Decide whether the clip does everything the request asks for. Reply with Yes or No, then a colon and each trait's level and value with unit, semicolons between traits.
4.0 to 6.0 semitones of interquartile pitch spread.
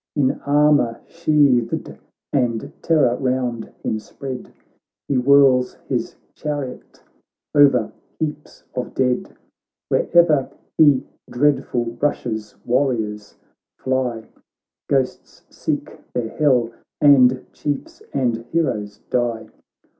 No: average, 3.3 semitones